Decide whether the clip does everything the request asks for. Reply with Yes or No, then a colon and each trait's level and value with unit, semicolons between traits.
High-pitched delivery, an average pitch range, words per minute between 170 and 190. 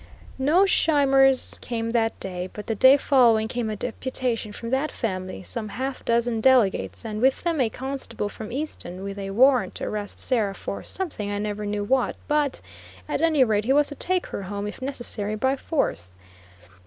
Yes: high, 235 Hz; average, 4.4 semitones; average, 185 wpm